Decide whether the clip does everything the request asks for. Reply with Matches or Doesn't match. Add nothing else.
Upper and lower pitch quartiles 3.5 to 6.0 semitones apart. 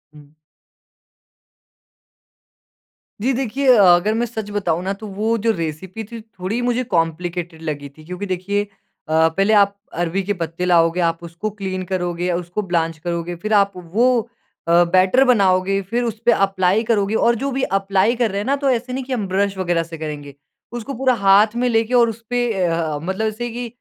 Matches